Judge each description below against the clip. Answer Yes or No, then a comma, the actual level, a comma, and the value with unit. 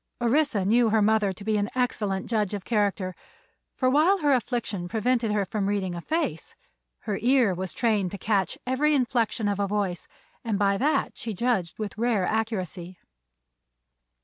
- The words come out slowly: No, average, 170 wpm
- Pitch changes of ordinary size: Yes, average, 3.6 semitones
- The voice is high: Yes, high, 215 Hz